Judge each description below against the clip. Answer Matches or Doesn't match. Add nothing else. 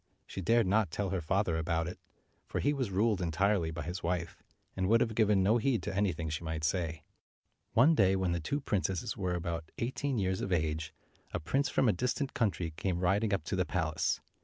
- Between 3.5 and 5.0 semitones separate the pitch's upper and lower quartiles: Matches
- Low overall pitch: Matches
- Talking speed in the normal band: Doesn't match